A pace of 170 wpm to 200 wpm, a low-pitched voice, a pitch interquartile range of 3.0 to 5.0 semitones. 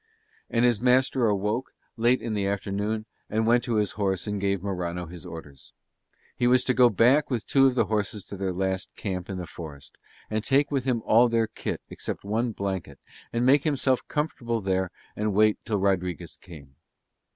Yes: average, 190 wpm; low, 105 Hz; average, 4.2 semitones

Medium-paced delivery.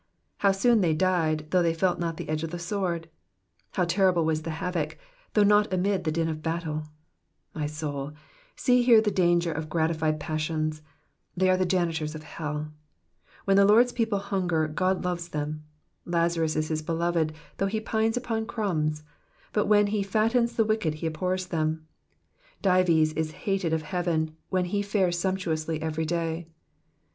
Yes: average, 170 wpm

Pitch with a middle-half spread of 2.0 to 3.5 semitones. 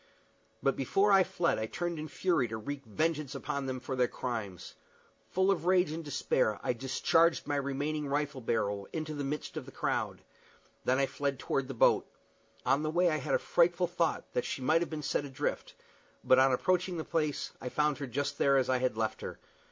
No: average, 4.0 semitones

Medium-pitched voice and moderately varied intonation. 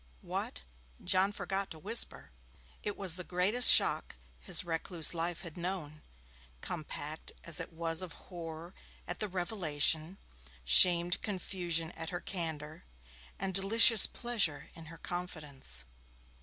Yes: medium, 175 Hz; average, 3.1 semitones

